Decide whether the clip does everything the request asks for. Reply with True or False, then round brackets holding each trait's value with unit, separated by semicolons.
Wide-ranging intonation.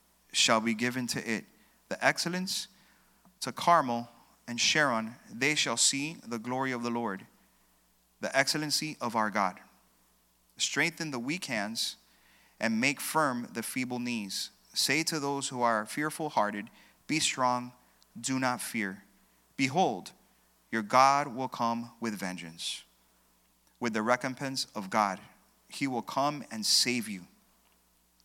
True (5.9 semitones)